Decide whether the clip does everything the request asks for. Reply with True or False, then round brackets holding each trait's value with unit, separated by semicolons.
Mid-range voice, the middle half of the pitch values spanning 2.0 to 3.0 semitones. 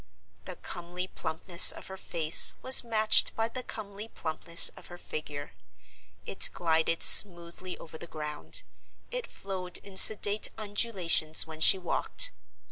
False (180 Hz; 4.2 semitones)